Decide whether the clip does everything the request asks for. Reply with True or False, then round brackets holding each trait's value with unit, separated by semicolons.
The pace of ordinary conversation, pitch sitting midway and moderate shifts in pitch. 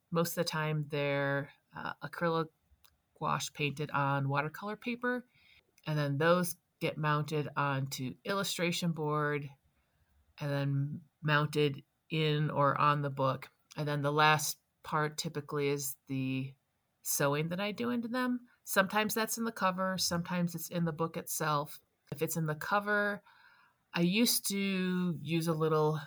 True (145 wpm; 155 Hz; 3.8 semitones)